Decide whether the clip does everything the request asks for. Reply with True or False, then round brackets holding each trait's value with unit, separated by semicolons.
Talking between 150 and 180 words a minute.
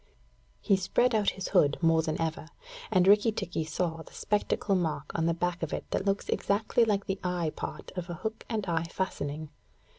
False (200 wpm)